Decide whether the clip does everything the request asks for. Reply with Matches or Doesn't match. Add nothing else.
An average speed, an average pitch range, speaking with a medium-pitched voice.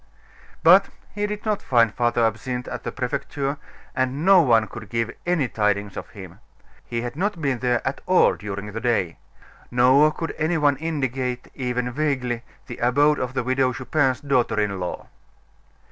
Doesn't match